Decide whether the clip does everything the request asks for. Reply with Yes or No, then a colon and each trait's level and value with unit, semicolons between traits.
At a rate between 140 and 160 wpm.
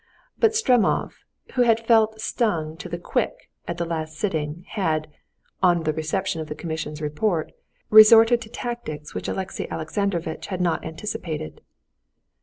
Yes: average, 145 wpm